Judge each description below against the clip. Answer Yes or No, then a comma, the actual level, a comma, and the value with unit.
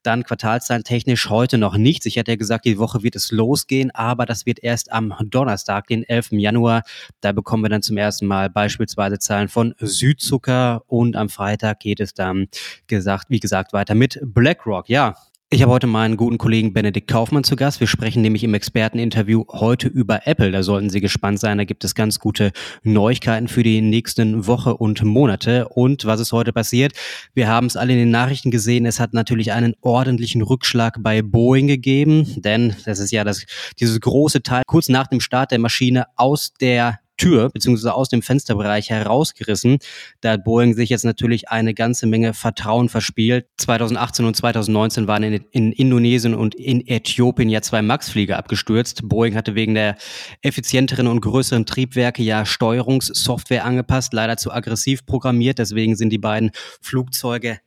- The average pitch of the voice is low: Yes, low, 115 Hz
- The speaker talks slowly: No, average, 180 wpm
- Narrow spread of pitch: Yes, narrow, 2.3 semitones